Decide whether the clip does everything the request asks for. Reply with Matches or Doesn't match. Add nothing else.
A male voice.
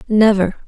Doesn't match